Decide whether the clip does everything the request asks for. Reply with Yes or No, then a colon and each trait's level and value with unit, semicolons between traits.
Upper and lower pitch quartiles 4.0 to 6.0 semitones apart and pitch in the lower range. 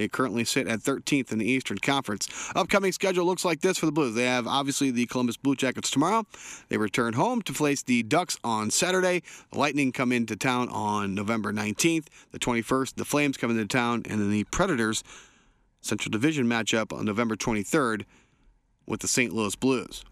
Yes: average, 4.5 semitones; low, 125 Hz